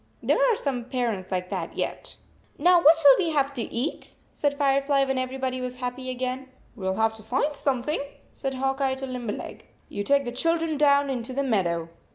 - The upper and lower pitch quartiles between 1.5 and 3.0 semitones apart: Yes, average, 2.7 semitones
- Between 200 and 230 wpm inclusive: Yes, fast, 205 wpm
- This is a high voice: Yes, very high, 260 Hz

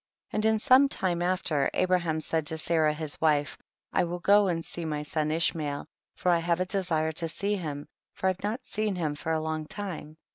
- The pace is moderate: No, fast, 225 wpm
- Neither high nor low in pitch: Yes, medium, 165 Hz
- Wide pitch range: No, average, 3.0 semitones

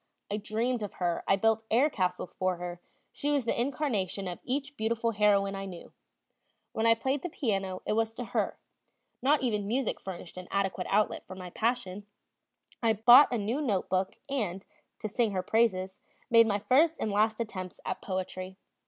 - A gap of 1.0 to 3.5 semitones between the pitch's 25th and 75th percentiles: No, average, 4.0 semitones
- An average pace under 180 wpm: No, average, 185 wpm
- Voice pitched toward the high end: Yes, high, 215 Hz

